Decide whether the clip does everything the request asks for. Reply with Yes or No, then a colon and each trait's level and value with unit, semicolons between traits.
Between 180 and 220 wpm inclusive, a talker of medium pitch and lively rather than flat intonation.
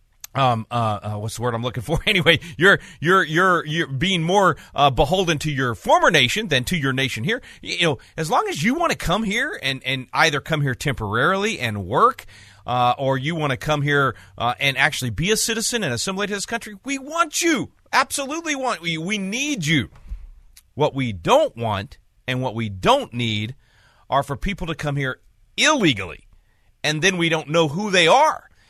Yes: average, 200 wpm; medium, 145 Hz; wide, 7.4 semitones